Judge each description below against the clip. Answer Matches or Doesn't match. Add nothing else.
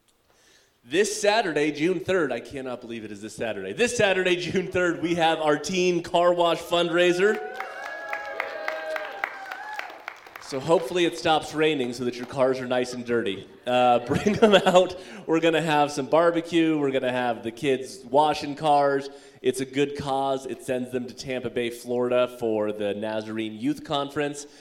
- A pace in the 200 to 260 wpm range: Doesn't match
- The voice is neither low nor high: Matches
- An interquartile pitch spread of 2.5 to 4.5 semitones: Doesn't match